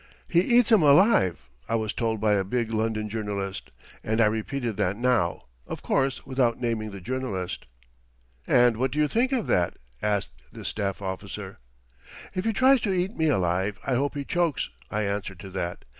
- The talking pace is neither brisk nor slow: Yes, average, 185 wpm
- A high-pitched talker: No, low, 115 Hz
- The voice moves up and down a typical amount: No, wide, 6.0 semitones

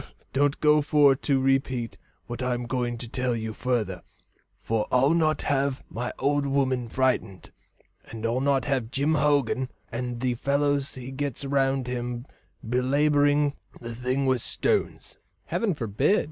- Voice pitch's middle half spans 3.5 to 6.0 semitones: No, average, 2.7 semitones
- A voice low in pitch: Yes, low, 130 Hz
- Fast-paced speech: No, average, 150 wpm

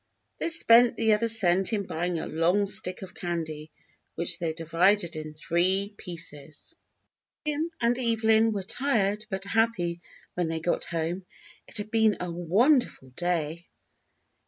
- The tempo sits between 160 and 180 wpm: No, average, 145 wpm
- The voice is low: No, medium, 185 Hz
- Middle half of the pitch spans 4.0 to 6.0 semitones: Yes, average, 4.8 semitones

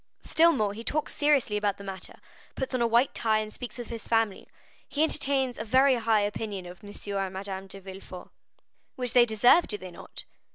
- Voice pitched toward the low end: No, high, 220 Hz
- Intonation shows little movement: No, average, 4.3 semitones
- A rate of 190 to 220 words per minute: Yes, fast, 205 wpm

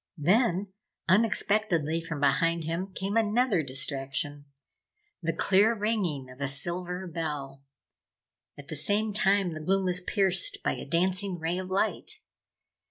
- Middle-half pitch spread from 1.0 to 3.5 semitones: No, average, 4.6 semitones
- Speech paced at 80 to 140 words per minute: Yes, slow, 135 wpm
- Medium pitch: Yes, medium, 180 Hz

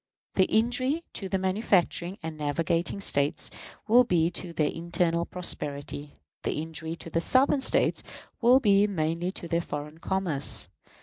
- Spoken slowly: No, average, 145 wpm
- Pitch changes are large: No, average, 3.7 semitones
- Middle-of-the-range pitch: Yes, medium, 170 Hz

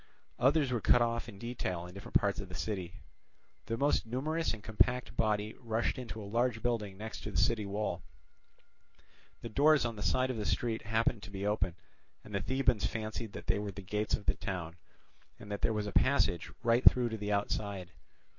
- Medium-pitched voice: No, low, 110 Hz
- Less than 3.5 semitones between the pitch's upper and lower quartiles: Yes, average, 2.8 semitones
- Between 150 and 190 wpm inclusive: No, fast, 205 wpm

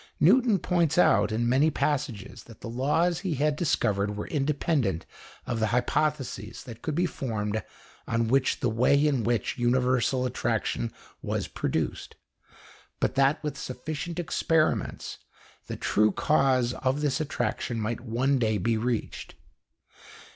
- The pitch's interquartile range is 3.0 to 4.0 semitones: No, average, 4.6 semitones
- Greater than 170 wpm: No, slow, 135 wpm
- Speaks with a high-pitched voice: No, low, 130 Hz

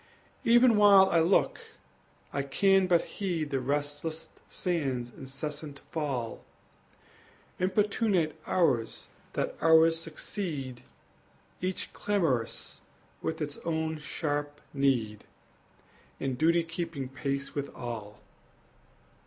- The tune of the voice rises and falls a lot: No, average, 4.0 semitones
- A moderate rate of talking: No, slow, 95 wpm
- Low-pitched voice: No, medium, 155 Hz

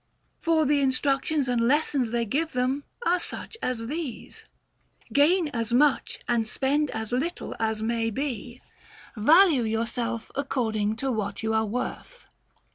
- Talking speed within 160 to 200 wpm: No, average, 140 wpm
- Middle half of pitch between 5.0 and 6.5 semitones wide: No, average, 4.3 semitones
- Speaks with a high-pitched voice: Yes, very high, 250 Hz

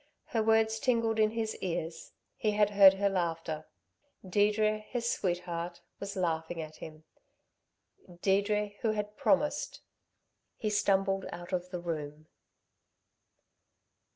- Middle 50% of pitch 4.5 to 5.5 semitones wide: No, average, 3.7 semitones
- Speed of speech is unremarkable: No, slow, 120 wpm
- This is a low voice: No, high, 195 Hz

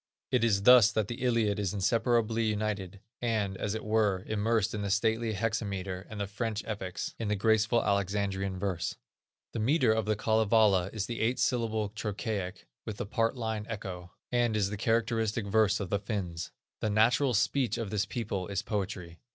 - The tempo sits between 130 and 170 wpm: No, average, 180 wpm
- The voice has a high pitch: No, low, 105 Hz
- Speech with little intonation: Yes, narrow, 2.2 semitones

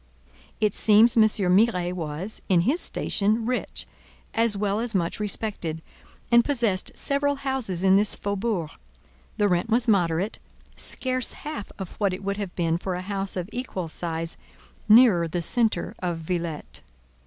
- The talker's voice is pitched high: Yes, high, 200 Hz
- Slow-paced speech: No, average, 155 wpm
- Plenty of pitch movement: No, average, 4.4 semitones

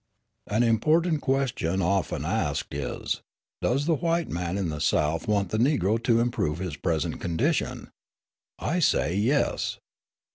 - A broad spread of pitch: Yes, wide, 8.1 semitones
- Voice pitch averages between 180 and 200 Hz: No, low, 105 Hz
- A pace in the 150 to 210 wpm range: No, average, 140 wpm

